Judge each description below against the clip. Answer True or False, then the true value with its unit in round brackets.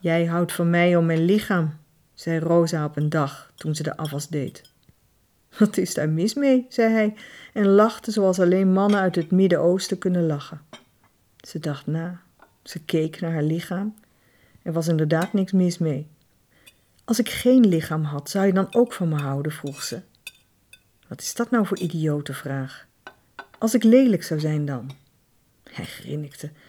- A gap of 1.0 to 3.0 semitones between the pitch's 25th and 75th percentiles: False (4.3 semitones)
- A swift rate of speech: False (175 wpm)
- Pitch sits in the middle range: True (170 Hz)